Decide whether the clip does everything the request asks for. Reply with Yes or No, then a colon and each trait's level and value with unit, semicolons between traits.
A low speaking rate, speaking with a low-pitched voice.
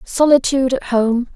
No: slow, 130 wpm; very high, 255 Hz